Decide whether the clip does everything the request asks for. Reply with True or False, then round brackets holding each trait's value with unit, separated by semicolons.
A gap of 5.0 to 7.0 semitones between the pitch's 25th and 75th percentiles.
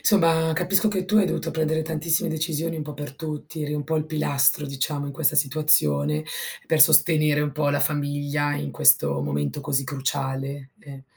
False (2.4 semitones)